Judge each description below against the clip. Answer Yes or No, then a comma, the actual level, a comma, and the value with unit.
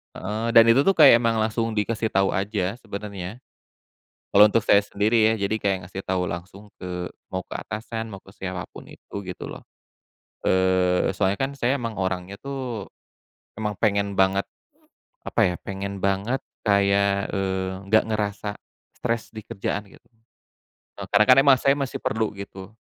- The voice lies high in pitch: No, low, 100 Hz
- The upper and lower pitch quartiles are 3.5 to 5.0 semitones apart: No, average, 2.8 semitones